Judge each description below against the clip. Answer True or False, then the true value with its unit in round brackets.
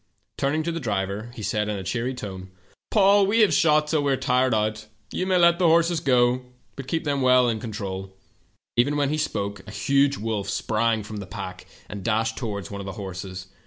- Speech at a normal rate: False (230 wpm)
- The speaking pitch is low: True (115 Hz)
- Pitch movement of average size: False (6.2 semitones)